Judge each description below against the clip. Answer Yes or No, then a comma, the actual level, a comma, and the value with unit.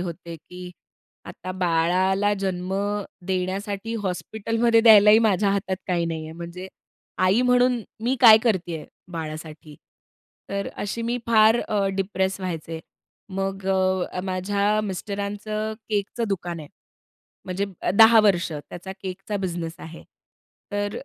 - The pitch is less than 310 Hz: Yes, high, 190 Hz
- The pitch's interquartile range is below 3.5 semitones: Yes, average, 3.0 semitones